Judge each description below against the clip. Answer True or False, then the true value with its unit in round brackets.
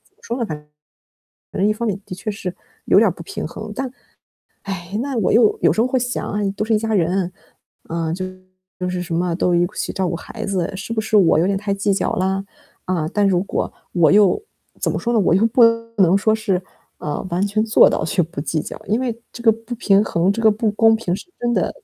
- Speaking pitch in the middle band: False (200 Hz)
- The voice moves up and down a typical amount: True (3.6 semitones)